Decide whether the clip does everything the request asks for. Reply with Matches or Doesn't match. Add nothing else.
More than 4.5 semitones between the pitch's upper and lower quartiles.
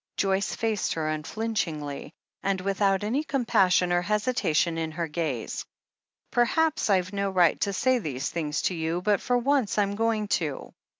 Matches